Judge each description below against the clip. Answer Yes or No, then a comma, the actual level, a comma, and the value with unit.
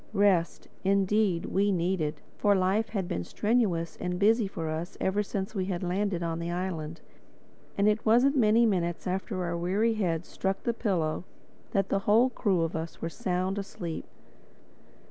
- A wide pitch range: No, average, 3.3 semitones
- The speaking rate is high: No, average, 165 wpm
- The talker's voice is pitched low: No, high, 190 Hz